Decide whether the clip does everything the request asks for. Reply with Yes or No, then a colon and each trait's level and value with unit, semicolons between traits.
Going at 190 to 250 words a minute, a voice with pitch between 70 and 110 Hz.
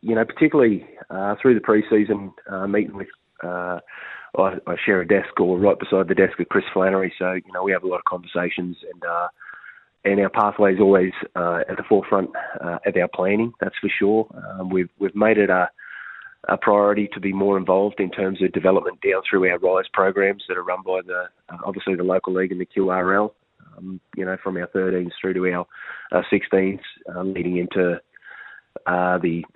Yes: average, 200 wpm; very low, 95 Hz